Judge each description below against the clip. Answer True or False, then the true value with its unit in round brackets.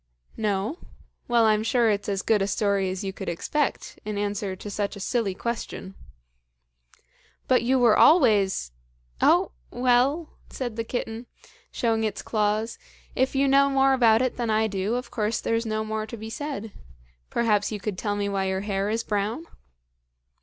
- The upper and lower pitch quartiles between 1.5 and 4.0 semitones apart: True (3.0 semitones)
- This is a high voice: True (220 Hz)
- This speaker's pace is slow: False (175 wpm)